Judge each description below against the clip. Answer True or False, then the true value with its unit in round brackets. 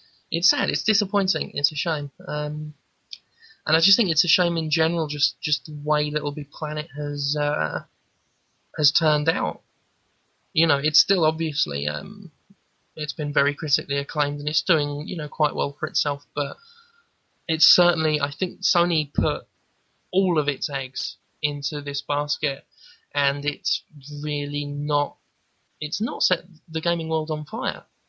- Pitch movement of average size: False (2.3 semitones)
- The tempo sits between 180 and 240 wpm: False (160 wpm)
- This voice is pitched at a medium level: True (150 Hz)